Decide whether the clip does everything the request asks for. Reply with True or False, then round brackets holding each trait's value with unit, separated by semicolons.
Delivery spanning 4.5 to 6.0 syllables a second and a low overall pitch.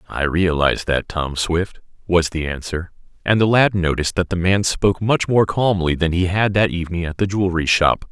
True (5.3 syllables/s; 90 Hz)